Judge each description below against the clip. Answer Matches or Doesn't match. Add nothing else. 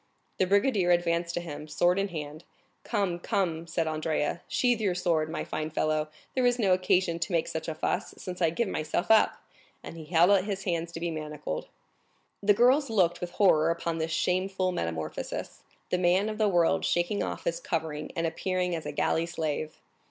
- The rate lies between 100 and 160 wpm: Doesn't match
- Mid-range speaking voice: Matches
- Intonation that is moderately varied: Matches